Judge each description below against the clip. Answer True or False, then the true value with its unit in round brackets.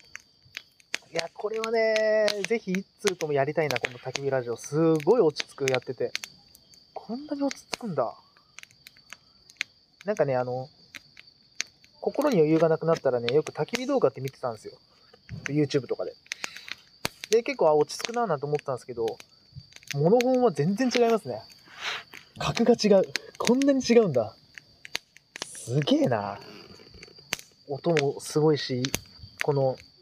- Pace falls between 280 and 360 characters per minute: True (295 characters per minute)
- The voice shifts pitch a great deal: True (8.4 semitones)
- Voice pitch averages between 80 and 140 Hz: False (160 Hz)